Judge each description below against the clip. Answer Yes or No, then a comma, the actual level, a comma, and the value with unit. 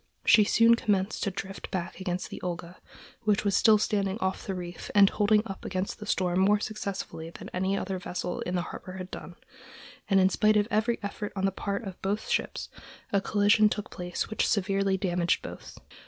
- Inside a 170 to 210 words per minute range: Yes, average, 200 wpm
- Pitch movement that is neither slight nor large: No, narrow, 2.1 semitones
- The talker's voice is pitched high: Yes, high, 195 Hz